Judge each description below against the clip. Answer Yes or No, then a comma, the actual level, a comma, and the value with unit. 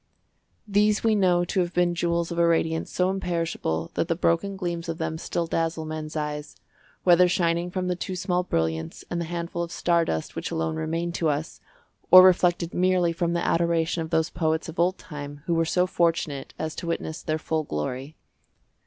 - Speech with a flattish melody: Yes, narrow, 1.8 semitones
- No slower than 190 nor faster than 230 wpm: Yes, average, 195 wpm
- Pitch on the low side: No, medium, 170 Hz